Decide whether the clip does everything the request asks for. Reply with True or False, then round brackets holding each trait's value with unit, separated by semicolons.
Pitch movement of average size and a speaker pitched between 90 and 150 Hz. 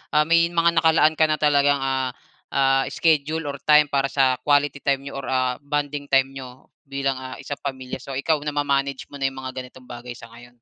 False (1.9 semitones; 140 Hz)